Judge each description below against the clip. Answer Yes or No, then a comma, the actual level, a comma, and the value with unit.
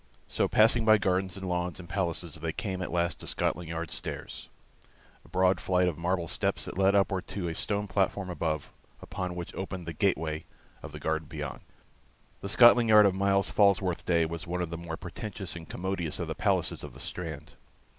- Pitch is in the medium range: No, very low, 90 Hz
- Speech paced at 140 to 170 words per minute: No, fast, 205 wpm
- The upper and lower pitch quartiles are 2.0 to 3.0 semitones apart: Yes, average, 2.7 semitones